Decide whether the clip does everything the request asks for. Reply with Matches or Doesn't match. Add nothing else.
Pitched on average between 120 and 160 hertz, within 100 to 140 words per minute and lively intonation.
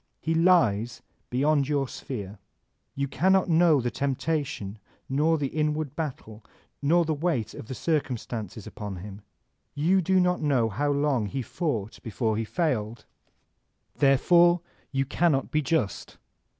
Matches